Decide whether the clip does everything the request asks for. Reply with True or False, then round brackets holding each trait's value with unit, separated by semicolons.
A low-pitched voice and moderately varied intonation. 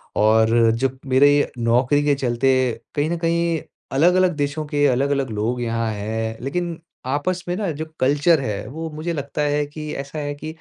False (145 Hz; 4.3 semitones)